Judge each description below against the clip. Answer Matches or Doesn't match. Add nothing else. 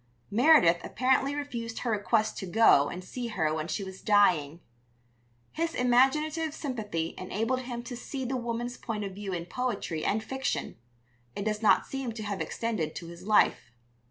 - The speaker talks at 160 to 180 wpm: Matches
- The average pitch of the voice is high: Matches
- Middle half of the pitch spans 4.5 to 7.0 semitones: Matches